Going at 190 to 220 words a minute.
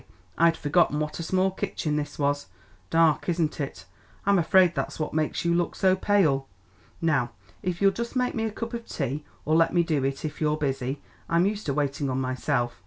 Yes: fast, 205 wpm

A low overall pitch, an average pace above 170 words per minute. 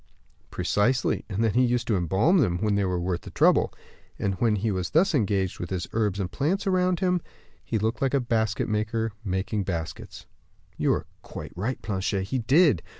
Yes: low, 110 Hz; average, 190 wpm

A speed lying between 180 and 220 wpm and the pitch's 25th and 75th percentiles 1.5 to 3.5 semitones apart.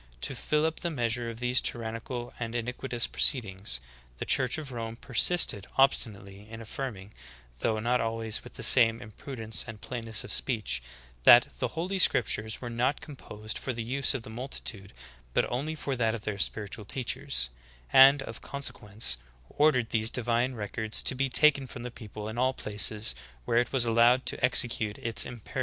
Yes: average, 185 wpm; average, 3.0 semitones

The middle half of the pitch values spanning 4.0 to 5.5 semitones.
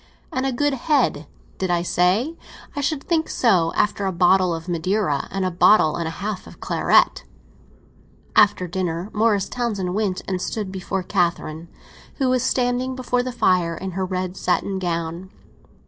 Yes: average, 5.2 semitones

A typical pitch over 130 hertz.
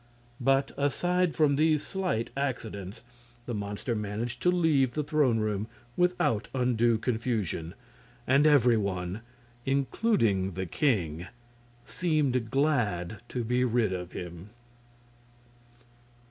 No: low, 120 Hz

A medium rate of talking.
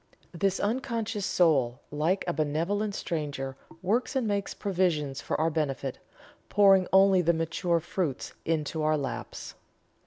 No: slow, 130 wpm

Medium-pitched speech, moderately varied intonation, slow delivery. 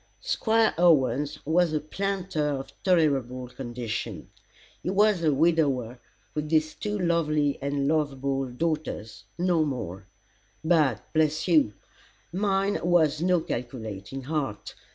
Yes: medium, 150 Hz; average, 4.4 semitones; slow, 115 wpm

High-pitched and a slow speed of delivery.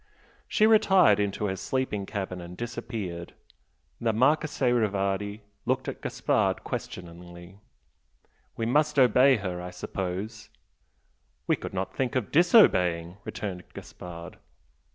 No: low, 105 Hz; slow, 115 wpm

